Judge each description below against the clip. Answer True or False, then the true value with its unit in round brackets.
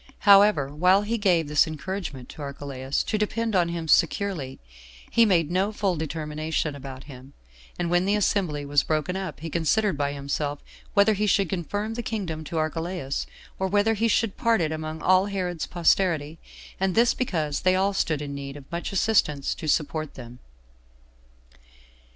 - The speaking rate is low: False (170 wpm)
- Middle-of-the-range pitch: True (170 Hz)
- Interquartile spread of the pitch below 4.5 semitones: False (5.1 semitones)